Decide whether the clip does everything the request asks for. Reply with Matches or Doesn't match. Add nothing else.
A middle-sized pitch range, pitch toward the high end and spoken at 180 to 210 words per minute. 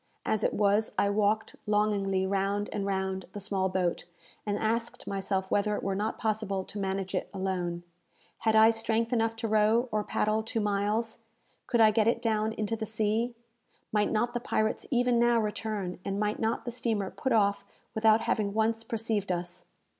Doesn't match